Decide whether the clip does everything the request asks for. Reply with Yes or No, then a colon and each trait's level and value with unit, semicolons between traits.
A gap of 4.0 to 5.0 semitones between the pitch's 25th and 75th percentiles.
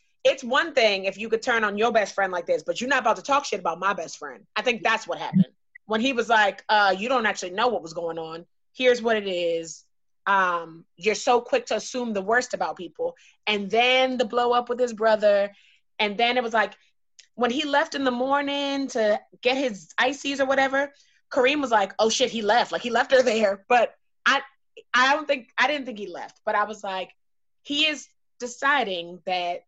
Yes: average, 4.6 semitones